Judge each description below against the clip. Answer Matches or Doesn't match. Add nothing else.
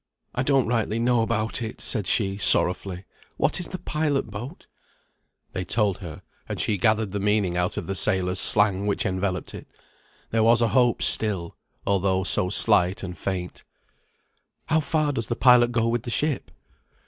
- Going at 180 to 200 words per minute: Doesn't match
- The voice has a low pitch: Matches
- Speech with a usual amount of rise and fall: Matches